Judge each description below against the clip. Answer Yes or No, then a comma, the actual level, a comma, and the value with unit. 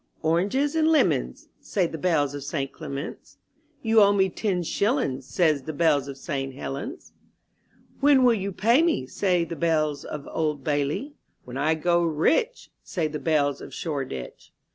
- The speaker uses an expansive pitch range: Yes, wide, 6.1 semitones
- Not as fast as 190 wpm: Yes, average, 165 wpm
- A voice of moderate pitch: Yes, medium, 160 Hz